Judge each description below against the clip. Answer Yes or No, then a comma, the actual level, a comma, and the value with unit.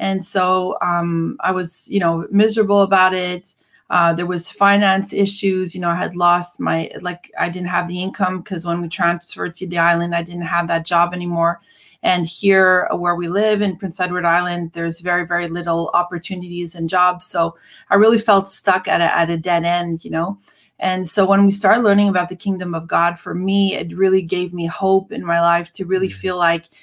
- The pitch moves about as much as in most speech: No, narrow, 2.0 semitones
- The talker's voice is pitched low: No, medium, 180 Hz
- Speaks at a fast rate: Yes, fast, 210 wpm